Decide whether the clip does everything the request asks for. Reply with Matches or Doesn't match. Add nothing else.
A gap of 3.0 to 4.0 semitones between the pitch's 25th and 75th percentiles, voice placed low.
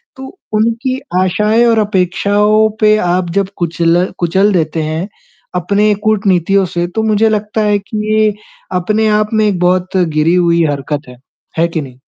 Doesn't match